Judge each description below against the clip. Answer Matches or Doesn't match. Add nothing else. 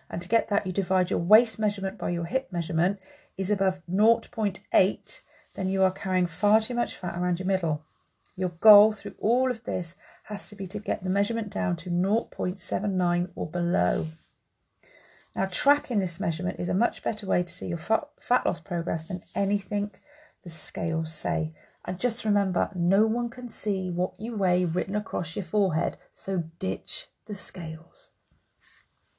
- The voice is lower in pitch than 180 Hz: Doesn't match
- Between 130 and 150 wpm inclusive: Doesn't match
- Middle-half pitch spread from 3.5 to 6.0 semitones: Doesn't match